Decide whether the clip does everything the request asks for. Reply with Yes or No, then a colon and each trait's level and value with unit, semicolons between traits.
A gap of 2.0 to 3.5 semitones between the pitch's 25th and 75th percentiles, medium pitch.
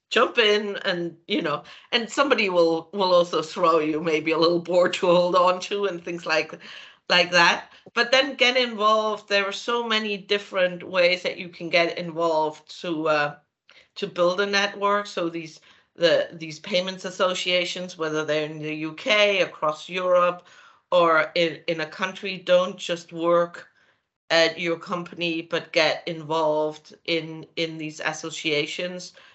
Yes: average, 2.9 semitones; medium, 175 Hz